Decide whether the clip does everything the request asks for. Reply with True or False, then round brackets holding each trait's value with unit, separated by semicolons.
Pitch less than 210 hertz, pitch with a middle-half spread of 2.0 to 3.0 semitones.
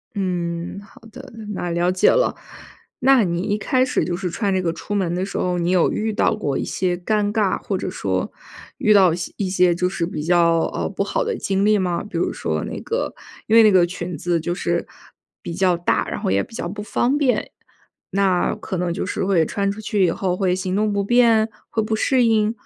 False (190 Hz; 3.4 semitones)